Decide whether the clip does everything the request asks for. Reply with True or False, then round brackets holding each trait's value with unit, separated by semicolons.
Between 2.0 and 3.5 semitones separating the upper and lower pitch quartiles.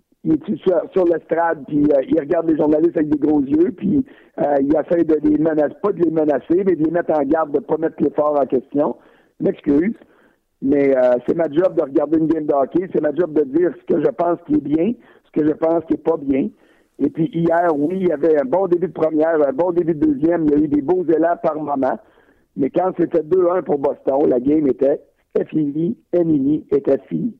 True (2.7 semitones)